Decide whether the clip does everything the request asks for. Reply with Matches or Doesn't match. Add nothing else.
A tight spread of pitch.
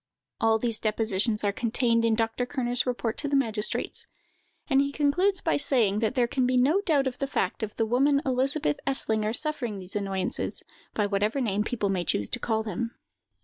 Doesn't match